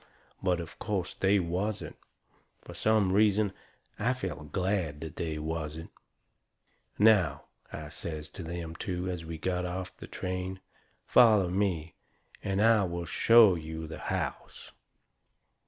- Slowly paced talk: Yes, slow, 130 wpm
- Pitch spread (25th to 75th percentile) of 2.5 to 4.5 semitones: Yes, average, 3.5 semitones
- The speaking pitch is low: Yes, very low, 90 Hz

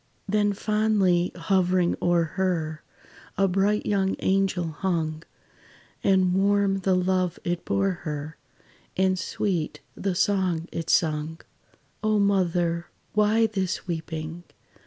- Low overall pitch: No, medium, 185 Hz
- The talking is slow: Yes, slow, 115 wpm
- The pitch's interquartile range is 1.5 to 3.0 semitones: Yes, narrow, 2.6 semitones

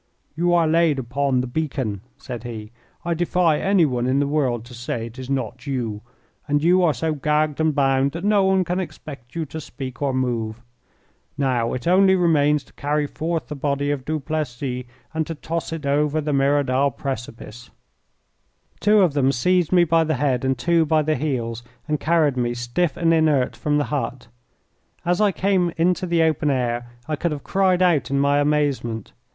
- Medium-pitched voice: Yes, medium, 145 Hz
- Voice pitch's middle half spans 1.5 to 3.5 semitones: No, average, 4.2 semitones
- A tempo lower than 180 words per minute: No, average, 190 wpm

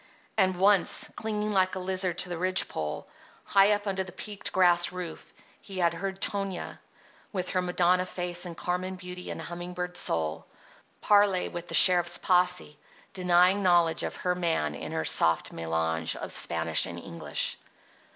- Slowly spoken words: No, average, 165 wpm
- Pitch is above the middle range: No, medium, 180 Hz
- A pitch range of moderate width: No, narrow, 1.7 semitones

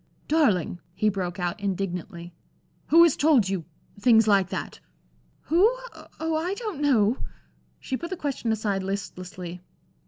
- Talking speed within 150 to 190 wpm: No, slow, 135 wpm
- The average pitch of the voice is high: Yes, high, 210 Hz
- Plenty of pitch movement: Yes, wide, 8.4 semitones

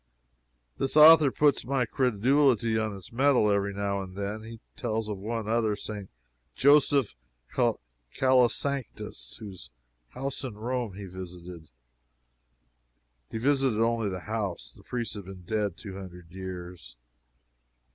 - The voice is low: Yes, low, 110 Hz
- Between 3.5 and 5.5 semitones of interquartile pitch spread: Yes, average, 4.7 semitones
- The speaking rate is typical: No, slow, 125 wpm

